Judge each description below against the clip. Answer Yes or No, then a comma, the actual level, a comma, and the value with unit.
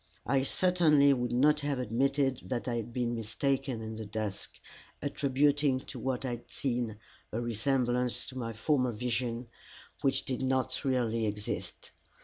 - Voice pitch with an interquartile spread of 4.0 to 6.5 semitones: No, average, 2.7 semitones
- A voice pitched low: Yes, low, 125 Hz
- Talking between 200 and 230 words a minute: No, average, 150 wpm